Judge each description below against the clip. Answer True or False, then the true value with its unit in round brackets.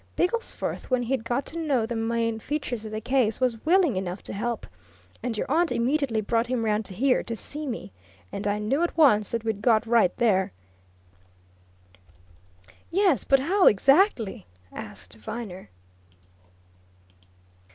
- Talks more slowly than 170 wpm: True (150 wpm)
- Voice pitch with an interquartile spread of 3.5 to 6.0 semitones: True (4.2 semitones)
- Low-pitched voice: False (235 Hz)